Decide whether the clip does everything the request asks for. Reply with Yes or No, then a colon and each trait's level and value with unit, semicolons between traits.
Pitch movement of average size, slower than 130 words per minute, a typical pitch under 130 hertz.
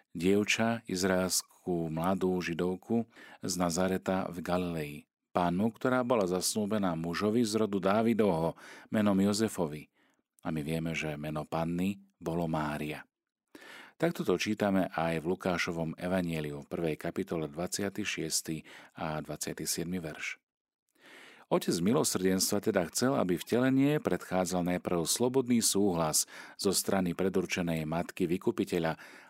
Yes: average, 3.5 semitones; average, 115 wpm; very low, 90 Hz